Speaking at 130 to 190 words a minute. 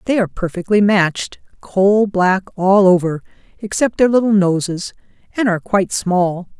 Yes: slow, 135 wpm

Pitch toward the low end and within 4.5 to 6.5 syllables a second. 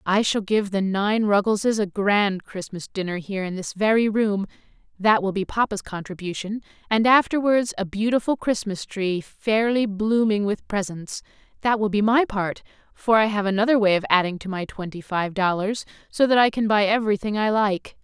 No: high, 205 Hz; 5.1 syllables/s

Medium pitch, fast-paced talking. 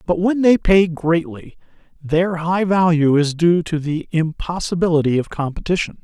No: medium, 170 Hz; average, 150 wpm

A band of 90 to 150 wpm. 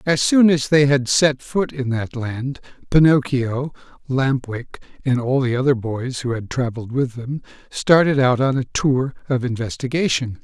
No: average, 175 wpm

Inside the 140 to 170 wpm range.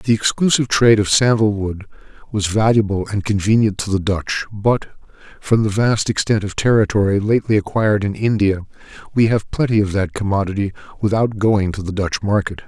Yes: average, 165 wpm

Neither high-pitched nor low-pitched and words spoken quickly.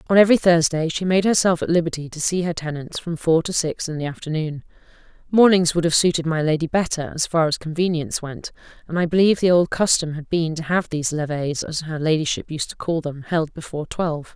Yes: medium, 165 Hz; fast, 220 wpm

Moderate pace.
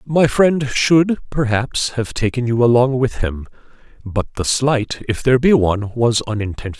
Yes: average, 170 wpm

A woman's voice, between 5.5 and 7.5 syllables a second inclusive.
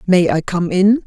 No: female; 4.4 syllables/s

